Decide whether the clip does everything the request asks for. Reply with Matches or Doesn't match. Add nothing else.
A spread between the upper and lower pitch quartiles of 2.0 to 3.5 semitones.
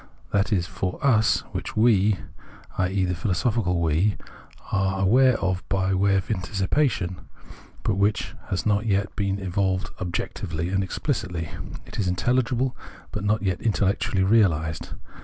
Matches